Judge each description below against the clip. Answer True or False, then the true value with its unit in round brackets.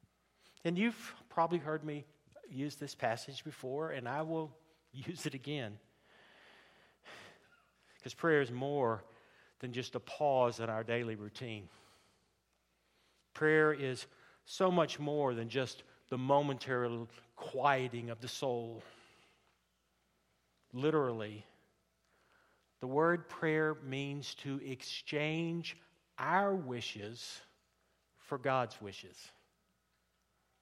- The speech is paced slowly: True (100 wpm)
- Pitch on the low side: True (130 Hz)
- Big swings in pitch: False (4.7 semitones)